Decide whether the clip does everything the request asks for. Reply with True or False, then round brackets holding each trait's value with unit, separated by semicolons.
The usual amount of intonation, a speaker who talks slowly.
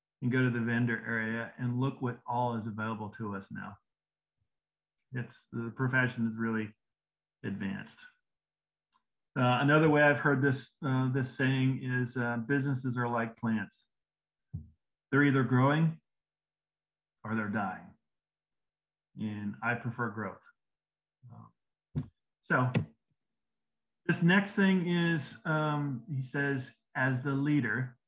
True (3.4 semitones; 120 wpm)